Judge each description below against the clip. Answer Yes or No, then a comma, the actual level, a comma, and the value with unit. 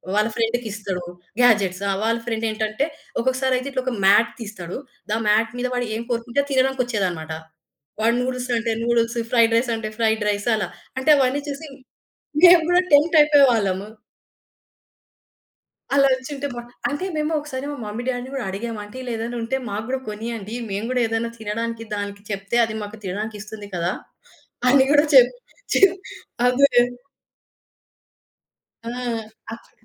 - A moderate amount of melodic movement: Yes, average, 3.5 semitones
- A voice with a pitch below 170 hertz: No, high, 230 Hz